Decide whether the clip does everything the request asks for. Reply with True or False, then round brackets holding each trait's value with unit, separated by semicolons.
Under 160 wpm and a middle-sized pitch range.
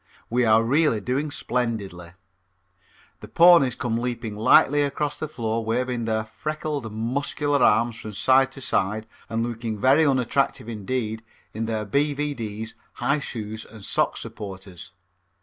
True (135 wpm; 4.0 semitones)